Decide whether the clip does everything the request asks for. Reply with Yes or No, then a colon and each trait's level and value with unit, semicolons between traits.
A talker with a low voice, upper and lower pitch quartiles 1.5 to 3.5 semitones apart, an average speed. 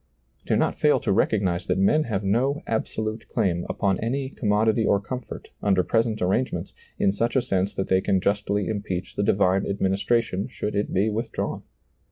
Yes: low, 105 Hz; average, 2.9 semitones; average, 180 wpm